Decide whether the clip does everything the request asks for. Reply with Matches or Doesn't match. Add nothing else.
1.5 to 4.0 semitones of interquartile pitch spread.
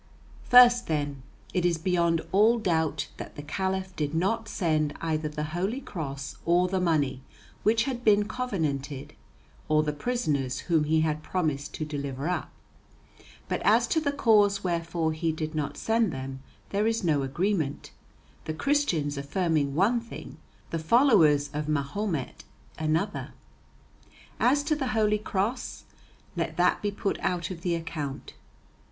Doesn't match